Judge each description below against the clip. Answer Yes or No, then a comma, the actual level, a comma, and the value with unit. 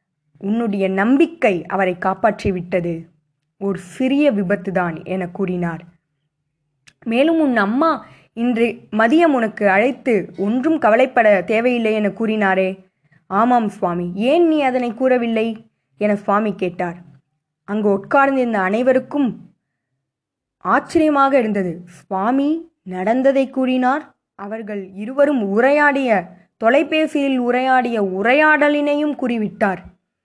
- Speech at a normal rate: Yes, average, 90 wpm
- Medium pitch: No, high, 215 Hz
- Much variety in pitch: Yes, wide, 5.9 semitones